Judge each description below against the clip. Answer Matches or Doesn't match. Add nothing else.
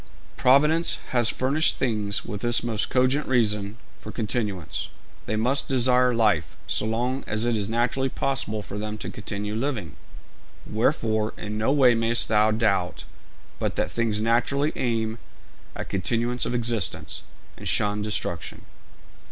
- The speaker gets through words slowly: Doesn't match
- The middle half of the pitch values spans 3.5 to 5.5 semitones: Doesn't match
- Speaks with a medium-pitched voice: Doesn't match